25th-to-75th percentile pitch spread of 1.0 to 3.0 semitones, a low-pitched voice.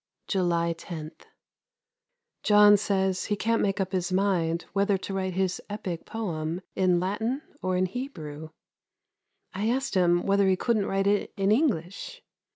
No: average, 2.7 semitones; high, 190 Hz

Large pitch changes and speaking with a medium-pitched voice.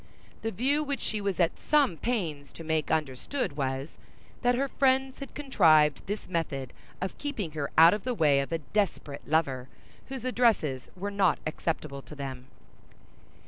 Yes: wide, 8.8 semitones; medium, 170 Hz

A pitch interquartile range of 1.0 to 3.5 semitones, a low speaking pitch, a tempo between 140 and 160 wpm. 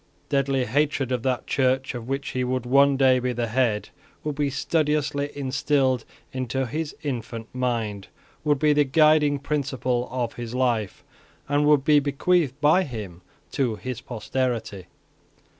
Yes: average, 2.8 semitones; low, 130 Hz; average, 150 wpm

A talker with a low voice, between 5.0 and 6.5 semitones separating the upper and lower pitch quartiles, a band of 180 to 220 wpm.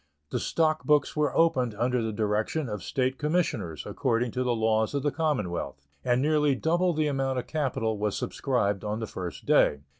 Yes: low, 125 Hz; wide, 5.5 semitones; average, 185 wpm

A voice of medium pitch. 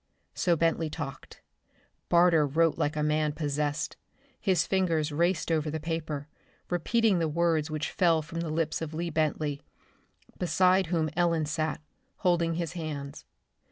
Yes: medium, 160 Hz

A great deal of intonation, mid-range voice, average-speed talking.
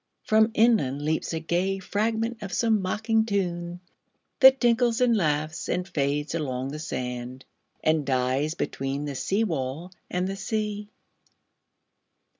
No: wide, 6.8 semitones; medium, 175 Hz; slow, 115 wpm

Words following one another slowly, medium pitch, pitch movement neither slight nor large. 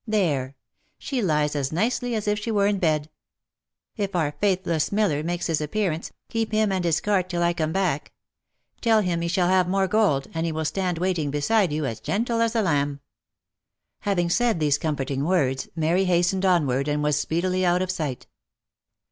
No: average, 190 wpm; medium, 175 Hz; average, 4.6 semitones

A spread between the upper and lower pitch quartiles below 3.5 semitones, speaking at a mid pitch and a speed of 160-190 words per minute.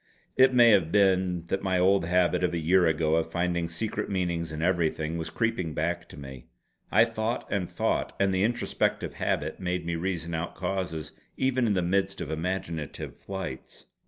No: average, 2.8 semitones; very low, 90 Hz; average, 185 wpm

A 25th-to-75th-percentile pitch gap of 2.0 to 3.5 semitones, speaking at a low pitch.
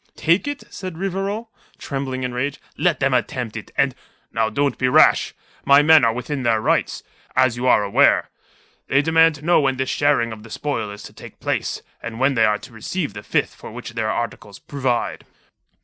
No: average, 4.5 semitones; low, 130 Hz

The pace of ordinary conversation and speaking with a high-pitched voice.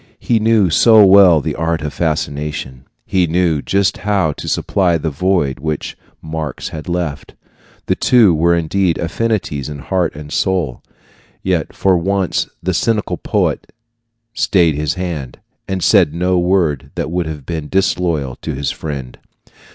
No: average, 150 wpm; very low, 85 Hz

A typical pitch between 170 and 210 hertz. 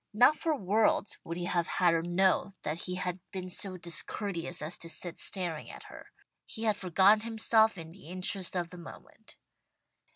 Yes: medium, 185 Hz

